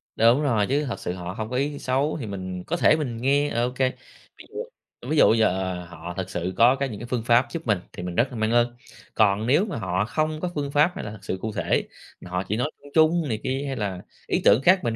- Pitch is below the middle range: Yes, low, 120 Hz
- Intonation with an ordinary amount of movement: No, wide, 5.9 semitones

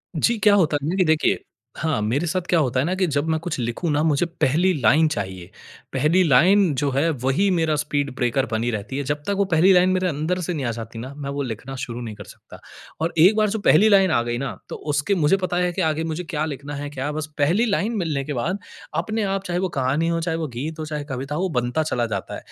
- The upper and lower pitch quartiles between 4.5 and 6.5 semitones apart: Yes, average, 4.9 semitones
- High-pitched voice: No, medium, 155 Hz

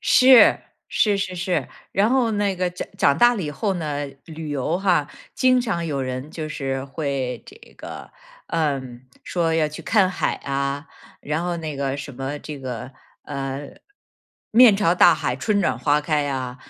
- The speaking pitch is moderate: Yes, medium, 155 Hz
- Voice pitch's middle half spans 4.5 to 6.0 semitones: Yes, average, 5.1 semitones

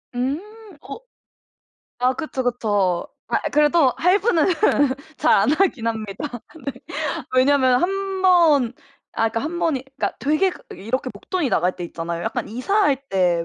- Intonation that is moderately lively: No, wide, 5.9 semitones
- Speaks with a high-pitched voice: Yes, very high, 255 Hz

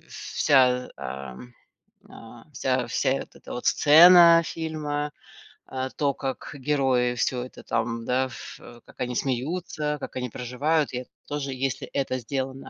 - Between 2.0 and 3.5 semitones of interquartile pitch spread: Yes, average, 2.9 semitones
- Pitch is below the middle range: Yes, low, 130 Hz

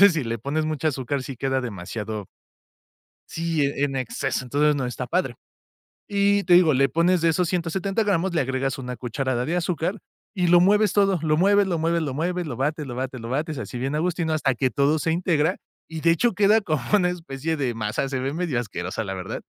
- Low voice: No, medium, 155 Hz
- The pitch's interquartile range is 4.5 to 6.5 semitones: Yes, average, 5.1 semitones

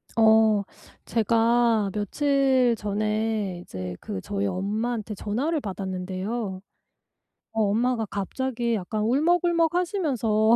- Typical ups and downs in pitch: Yes, average, 3.5 semitones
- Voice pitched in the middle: No, high, 220 Hz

